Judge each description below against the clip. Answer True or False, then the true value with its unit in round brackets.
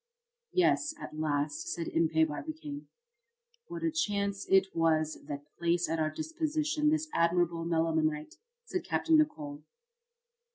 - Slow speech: True (125 wpm)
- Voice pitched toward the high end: False (170 Hz)